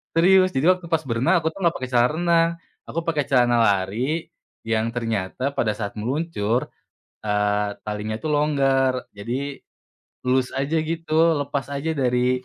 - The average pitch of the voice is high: No, low, 135 Hz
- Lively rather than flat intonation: Yes, wide, 5.7 semitones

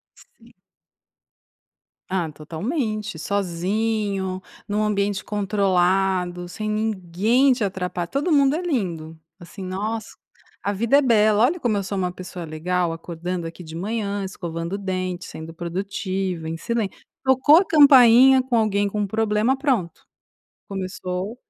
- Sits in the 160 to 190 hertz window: No, high, 200 Hz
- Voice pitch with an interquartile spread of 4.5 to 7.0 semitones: No, average, 3.7 semitones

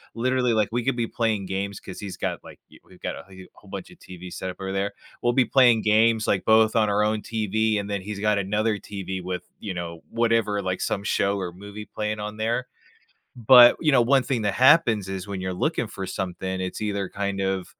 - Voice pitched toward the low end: Yes, low, 105 Hz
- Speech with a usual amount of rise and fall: Yes, average, 3.0 semitones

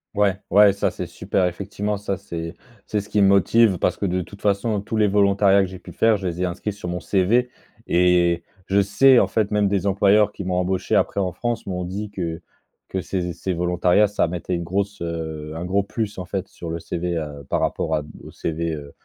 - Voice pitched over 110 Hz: No, very low, 95 Hz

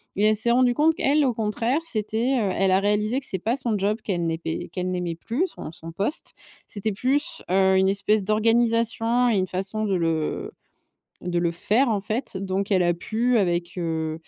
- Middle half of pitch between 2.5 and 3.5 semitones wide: No, average, 4.3 semitones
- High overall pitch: Yes, high, 210 Hz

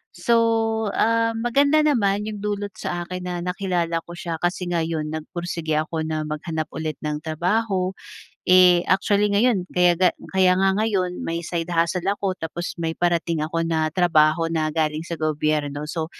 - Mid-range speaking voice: Yes, medium, 175 Hz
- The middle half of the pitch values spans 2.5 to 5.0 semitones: Yes, average, 3.7 semitones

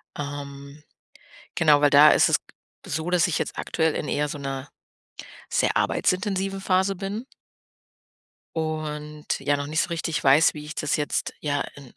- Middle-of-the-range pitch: Yes, medium, 150 Hz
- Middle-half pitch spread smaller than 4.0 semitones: Yes, average, 2.7 semitones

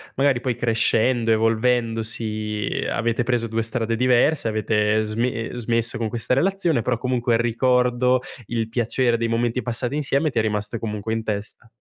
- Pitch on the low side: Yes, low, 115 Hz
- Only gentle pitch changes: Yes, narrow, 2.0 semitones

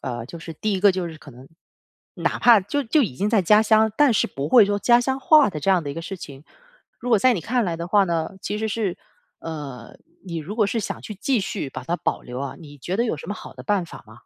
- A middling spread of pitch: No, wide, 6.0 semitones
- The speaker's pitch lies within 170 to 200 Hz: Yes, high, 190 Hz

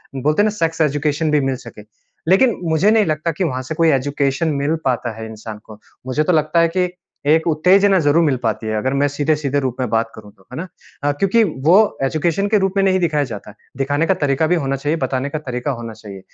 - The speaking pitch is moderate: Yes, medium, 150 Hz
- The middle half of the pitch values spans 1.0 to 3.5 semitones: No, average, 4.2 semitones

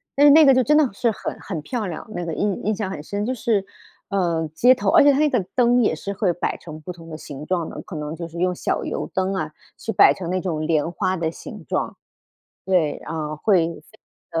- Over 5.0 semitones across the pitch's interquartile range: Yes, wide, 5.5 semitones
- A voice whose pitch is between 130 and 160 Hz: No, medium, 185 Hz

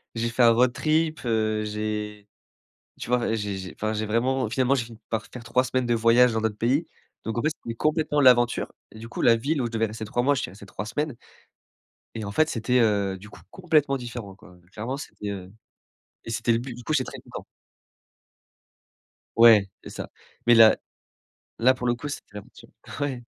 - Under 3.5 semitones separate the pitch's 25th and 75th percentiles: Yes, average, 3.0 semitones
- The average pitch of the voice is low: Yes, low, 115 Hz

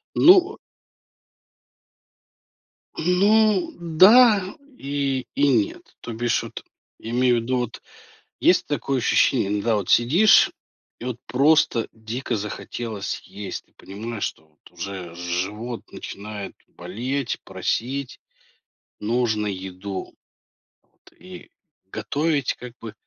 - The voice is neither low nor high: No, low, 120 Hz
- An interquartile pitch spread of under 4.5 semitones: No, wide, 5.4 semitones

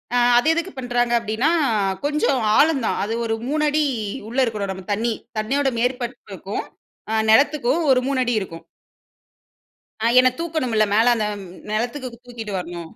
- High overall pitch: Yes, high, 240 Hz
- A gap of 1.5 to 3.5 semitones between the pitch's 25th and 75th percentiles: No, average, 4.0 semitones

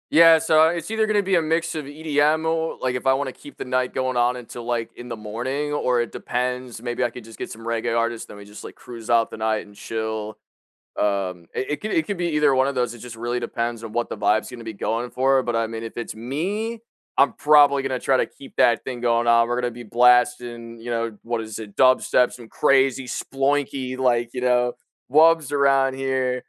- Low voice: Yes, low, 125 Hz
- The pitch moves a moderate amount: Yes, average, 3.2 semitones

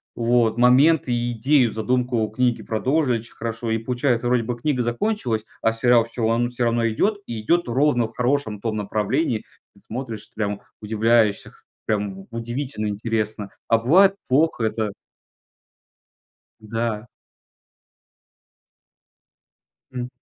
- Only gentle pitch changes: Yes, narrow, 2.2 semitones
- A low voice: Yes, low, 115 Hz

